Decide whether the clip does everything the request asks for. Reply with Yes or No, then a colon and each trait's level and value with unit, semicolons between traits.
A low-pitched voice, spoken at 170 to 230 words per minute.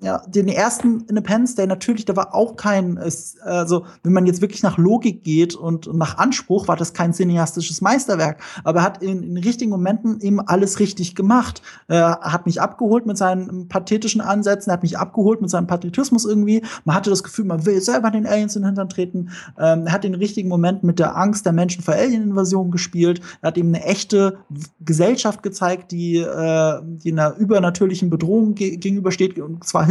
No: high, 190 Hz; fast, 190 wpm